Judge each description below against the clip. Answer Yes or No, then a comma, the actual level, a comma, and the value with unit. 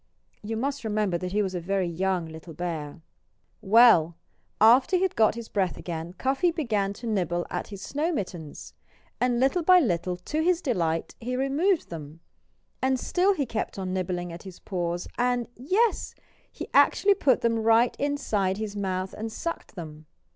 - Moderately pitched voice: No, high, 210 Hz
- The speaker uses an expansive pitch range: Yes, wide, 6.8 semitones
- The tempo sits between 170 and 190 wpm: Yes, average, 175 wpm